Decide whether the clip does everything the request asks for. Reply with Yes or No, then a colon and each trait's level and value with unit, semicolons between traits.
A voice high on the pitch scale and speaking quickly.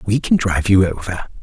No: very low, 95 Hz; fast, 210 wpm